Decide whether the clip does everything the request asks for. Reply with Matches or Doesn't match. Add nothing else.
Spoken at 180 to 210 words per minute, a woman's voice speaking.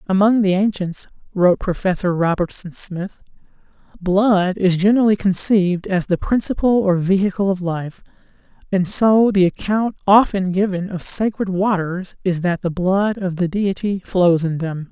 Doesn't match